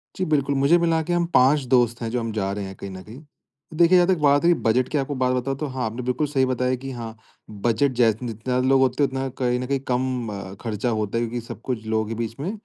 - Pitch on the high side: No, low, 125 Hz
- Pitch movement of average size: Yes, average, 3.5 semitones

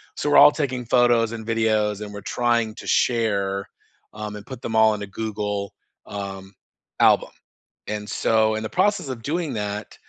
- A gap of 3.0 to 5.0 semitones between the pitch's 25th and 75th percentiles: No, narrow, 2.5 semitones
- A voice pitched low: Yes, low, 110 Hz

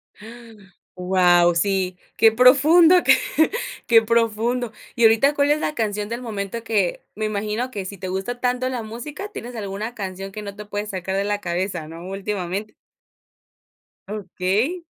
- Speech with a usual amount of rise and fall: Yes, average, 3.7 semitones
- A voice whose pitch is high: Yes, high, 210 Hz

